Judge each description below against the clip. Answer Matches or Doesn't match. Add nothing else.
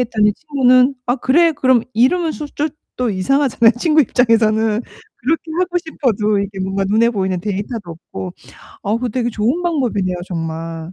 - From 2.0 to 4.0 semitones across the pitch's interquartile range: Doesn't match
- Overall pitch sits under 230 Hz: Doesn't match